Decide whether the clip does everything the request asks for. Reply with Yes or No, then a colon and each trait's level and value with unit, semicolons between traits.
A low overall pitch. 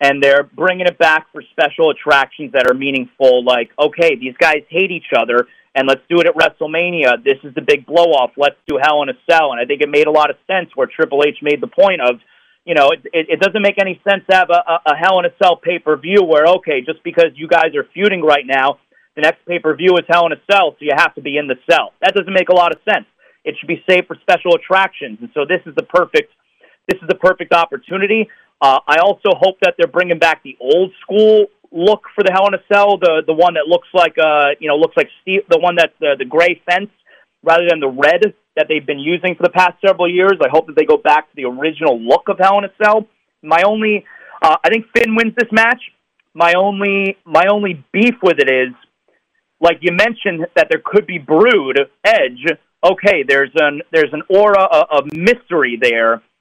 No: medium, 175 Hz